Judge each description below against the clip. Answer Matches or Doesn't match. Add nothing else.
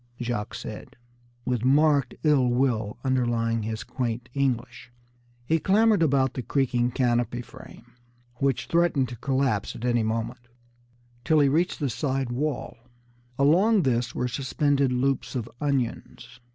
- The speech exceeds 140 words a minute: Doesn't match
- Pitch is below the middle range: Matches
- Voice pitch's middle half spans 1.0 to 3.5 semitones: Matches